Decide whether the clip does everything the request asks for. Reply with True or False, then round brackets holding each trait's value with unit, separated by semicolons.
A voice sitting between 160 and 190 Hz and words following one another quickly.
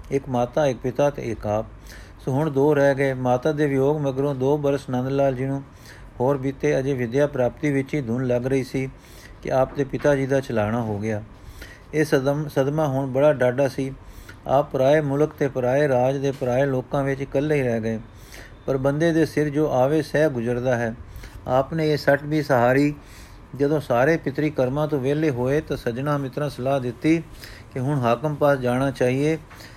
False (135 Hz; 190 wpm)